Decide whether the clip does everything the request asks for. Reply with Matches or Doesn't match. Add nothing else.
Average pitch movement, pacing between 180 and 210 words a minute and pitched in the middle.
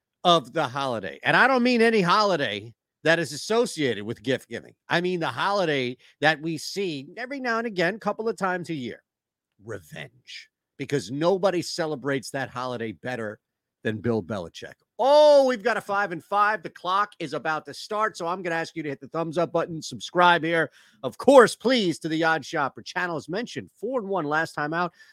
Doesn't match